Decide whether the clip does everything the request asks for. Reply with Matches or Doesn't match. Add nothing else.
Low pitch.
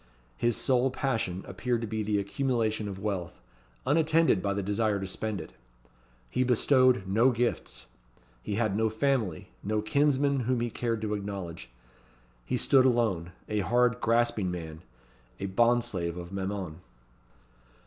Matches